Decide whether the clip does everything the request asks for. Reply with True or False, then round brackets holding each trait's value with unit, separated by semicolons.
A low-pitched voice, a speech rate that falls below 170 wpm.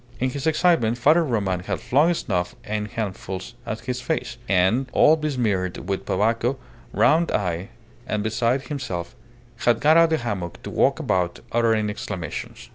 True (115 Hz; 160 wpm)